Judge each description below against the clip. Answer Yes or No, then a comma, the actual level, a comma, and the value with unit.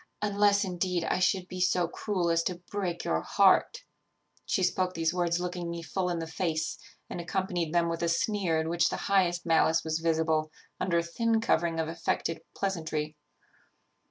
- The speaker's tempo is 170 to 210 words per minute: Yes, average, 180 wpm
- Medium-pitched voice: Yes, medium, 175 Hz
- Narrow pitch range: Yes, narrow, 2.1 semitones